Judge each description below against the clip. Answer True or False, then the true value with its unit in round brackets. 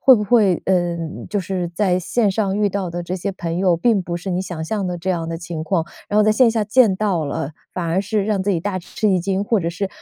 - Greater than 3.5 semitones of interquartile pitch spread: False (3.2 semitones)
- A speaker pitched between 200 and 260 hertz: False (190 Hz)